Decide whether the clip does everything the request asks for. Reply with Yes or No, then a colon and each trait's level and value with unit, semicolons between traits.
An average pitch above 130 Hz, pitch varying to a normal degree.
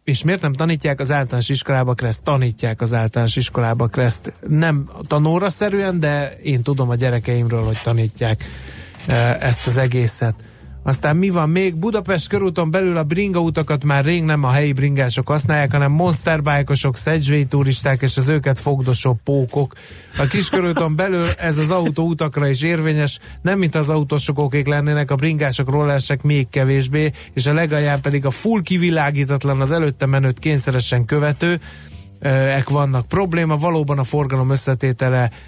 Yes: medium, 140 Hz; average, 3.3 semitones